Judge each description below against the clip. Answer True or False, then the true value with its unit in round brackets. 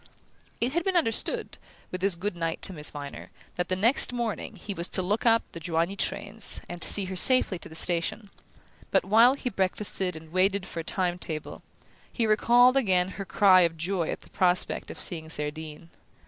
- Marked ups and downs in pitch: False (4.1 semitones)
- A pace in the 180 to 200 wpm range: True (195 wpm)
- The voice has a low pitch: False (185 Hz)